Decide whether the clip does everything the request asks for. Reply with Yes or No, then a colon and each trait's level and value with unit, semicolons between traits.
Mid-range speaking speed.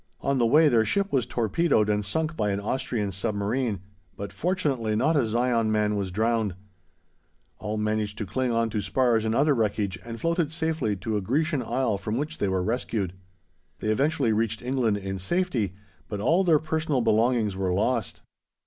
Yes: average, 180 wpm